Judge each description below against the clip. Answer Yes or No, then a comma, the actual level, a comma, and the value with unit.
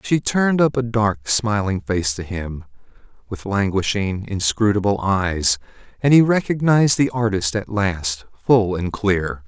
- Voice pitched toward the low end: Yes, low, 105 Hz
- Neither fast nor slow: Yes, average, 145 wpm